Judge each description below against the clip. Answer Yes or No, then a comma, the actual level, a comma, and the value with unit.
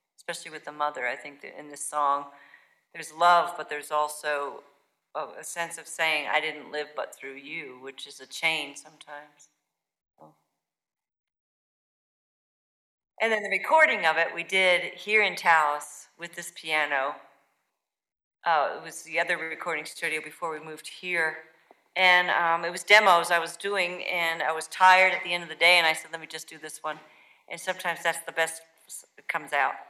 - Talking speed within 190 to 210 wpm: No, average, 180 wpm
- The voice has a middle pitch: Yes, medium, 160 Hz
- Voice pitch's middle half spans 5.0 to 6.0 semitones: No, narrow, 2.4 semitones